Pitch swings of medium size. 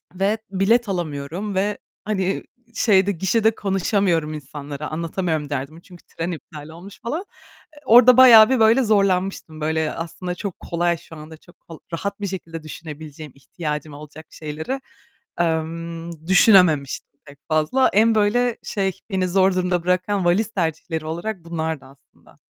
Yes: average, 4.1 semitones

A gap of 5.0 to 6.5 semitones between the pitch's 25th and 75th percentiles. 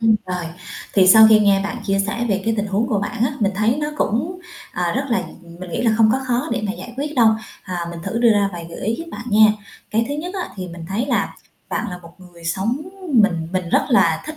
No: average, 4.5 semitones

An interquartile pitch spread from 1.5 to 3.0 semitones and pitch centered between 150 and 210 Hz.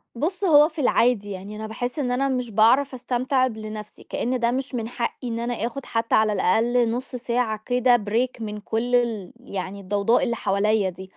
No: average, 2.7 semitones; high, 235 Hz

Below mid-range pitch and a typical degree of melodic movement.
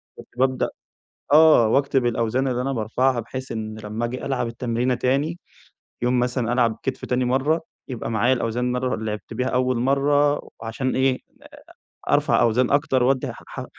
No: low, 125 Hz; narrow, 2.2 semitones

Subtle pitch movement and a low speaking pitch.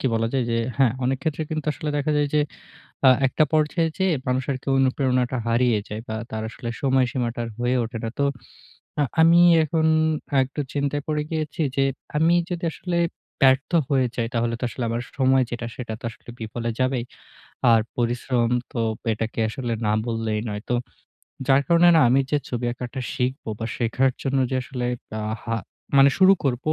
No: average, 3.6 semitones; low, 130 Hz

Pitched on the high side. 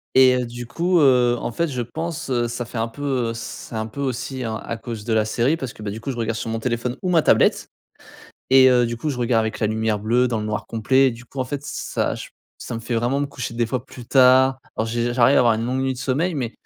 No: low, 120 Hz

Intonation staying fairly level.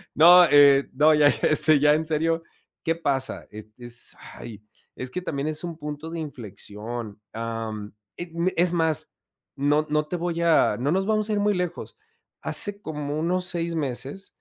No: average, 4.0 semitones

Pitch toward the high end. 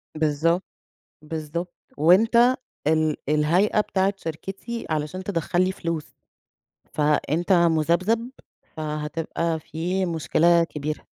No: medium, 165 Hz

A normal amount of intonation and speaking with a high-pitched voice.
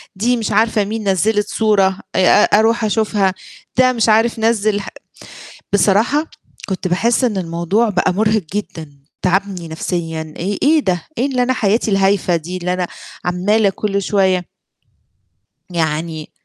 Yes: average, 3.5 semitones; high, 200 Hz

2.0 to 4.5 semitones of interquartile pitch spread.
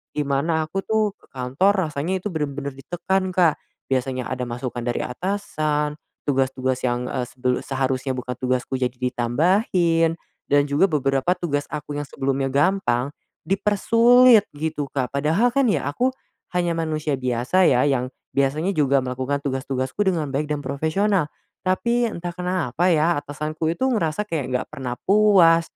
No: average, 5.3 semitones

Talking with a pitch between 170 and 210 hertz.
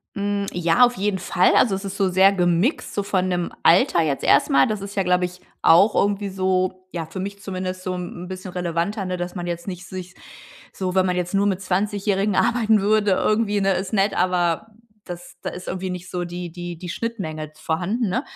Yes: medium, 185 Hz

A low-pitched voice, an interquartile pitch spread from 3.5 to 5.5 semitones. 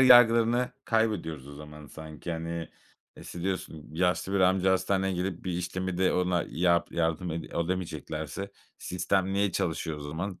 No: very low, 90 Hz; average, 2.8 semitones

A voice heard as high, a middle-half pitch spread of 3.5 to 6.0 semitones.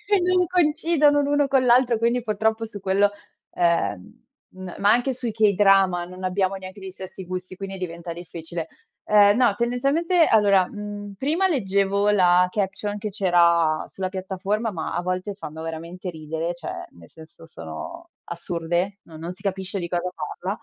Yes: high, 195 Hz; average, 4.2 semitones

